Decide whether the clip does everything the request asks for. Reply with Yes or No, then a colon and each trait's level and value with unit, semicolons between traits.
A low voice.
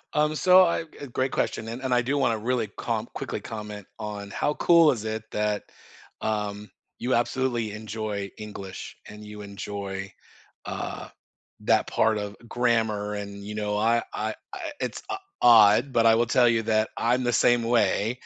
Yes: low, 110 Hz